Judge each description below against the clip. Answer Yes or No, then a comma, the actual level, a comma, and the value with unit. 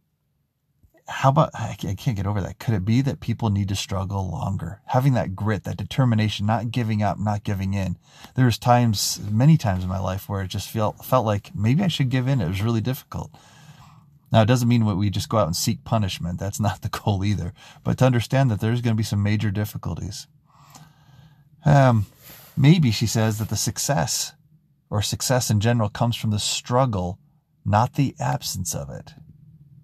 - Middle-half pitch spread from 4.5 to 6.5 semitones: Yes, average, 5.2 semitones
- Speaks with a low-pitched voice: Yes, low, 115 Hz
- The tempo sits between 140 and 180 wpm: No, average, 195 wpm